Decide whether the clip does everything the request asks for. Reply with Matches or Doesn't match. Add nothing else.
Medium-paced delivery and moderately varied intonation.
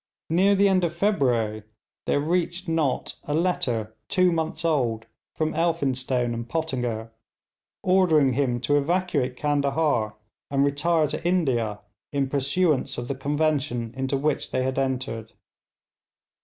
Doesn't match